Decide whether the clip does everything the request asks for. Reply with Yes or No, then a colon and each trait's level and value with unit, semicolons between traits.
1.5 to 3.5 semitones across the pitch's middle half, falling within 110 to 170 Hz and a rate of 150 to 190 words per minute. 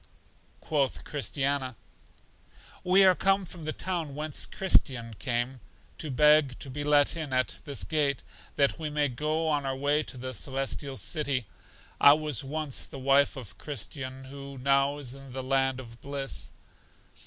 Yes: narrow, 2.4 semitones; medium, 140 Hz; average, 160 wpm